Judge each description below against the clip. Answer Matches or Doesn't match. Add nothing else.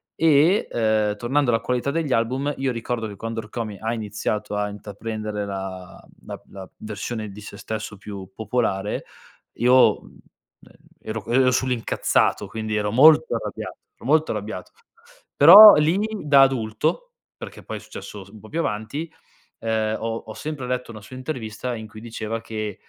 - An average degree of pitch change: Matches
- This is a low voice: Matches